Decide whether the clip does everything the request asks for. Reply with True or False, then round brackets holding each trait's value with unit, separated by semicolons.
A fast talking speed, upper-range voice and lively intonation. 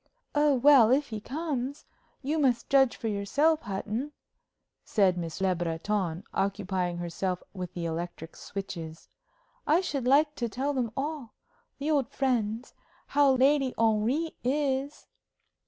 False (135 wpm; 240 Hz; 6.7 semitones)